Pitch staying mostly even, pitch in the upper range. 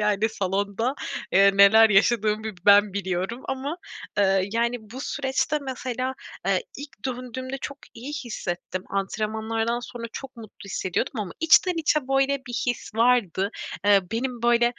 No: average, 4.3 semitones; high, 230 Hz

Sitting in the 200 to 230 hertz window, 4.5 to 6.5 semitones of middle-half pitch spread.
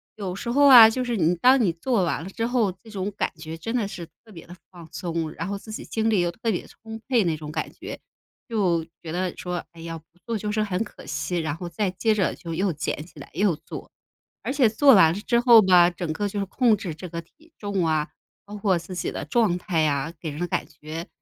No: medium, 185 Hz; average, 4.8 semitones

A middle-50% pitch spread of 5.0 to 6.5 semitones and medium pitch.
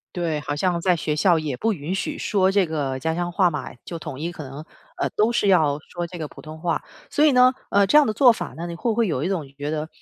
No: average, 4.2 semitones; medium, 170 Hz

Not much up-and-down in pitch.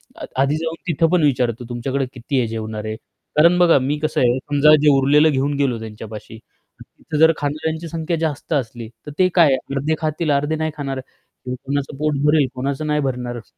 No: average, 3.8 semitones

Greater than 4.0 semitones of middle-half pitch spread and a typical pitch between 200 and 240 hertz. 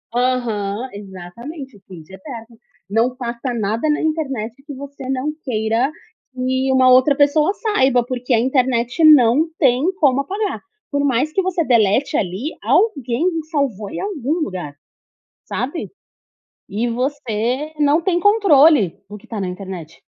No: average, 4.6 semitones; very high, 255 Hz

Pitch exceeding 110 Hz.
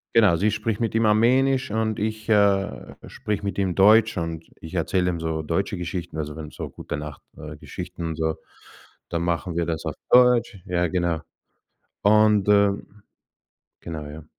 No: very low, 95 Hz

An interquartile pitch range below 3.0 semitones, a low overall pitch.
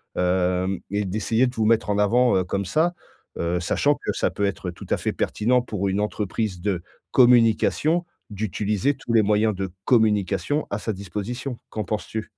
No: average, 3.3 semitones; low, 105 Hz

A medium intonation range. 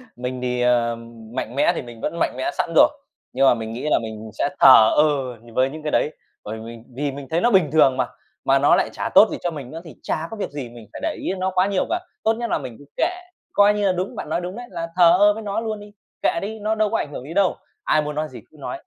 No: wide, 7.4 semitones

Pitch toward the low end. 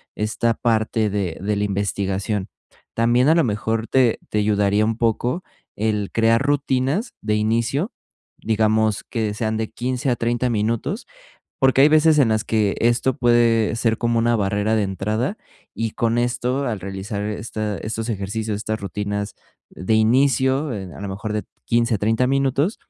Yes: low, 110 Hz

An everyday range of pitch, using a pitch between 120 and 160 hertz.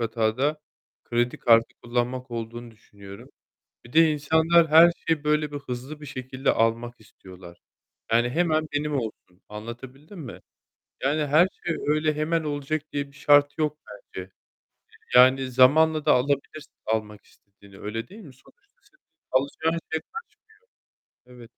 Yes: average, 4.6 semitones; low, 135 Hz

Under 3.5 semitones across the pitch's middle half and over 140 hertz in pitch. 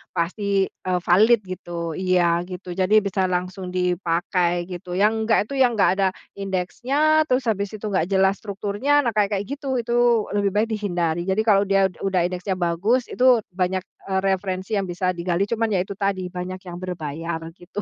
Yes: average, 2.8 semitones; high, 190 Hz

